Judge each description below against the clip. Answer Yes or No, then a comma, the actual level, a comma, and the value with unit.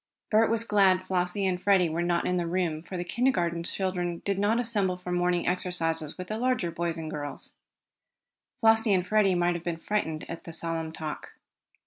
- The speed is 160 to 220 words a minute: Yes, average, 190 wpm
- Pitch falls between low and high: Yes, medium, 180 Hz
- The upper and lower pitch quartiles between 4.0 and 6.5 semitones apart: No, average, 2.9 semitones